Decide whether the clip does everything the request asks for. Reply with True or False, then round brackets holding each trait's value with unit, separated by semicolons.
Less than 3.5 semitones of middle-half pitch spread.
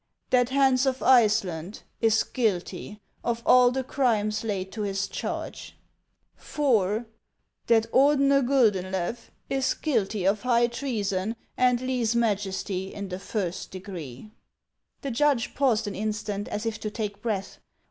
False (4.0 semitones)